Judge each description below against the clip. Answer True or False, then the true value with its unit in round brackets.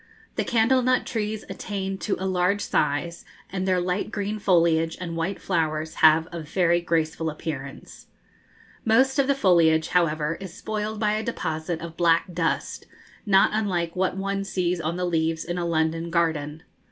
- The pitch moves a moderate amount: True (3.4 semitones)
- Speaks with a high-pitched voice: False (175 Hz)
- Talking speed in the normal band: True (165 wpm)